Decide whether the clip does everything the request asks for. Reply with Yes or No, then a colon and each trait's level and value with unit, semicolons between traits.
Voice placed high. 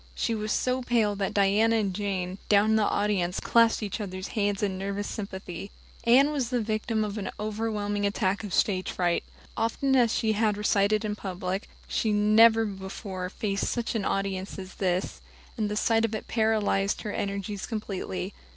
Yes: high, 205 Hz